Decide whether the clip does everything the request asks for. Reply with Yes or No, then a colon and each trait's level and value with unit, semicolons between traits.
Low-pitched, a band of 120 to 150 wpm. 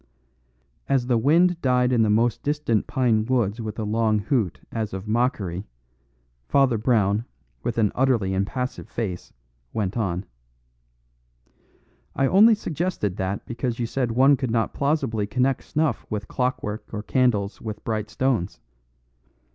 Yes: low, 115 Hz; average, 140 wpm